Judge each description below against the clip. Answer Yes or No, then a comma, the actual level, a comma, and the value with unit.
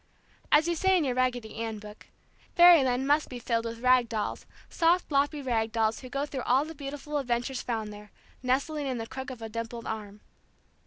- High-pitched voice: Yes, very high, 255 Hz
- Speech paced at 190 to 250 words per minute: Yes, average, 200 wpm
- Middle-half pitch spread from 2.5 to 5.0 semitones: Yes, average, 3.9 semitones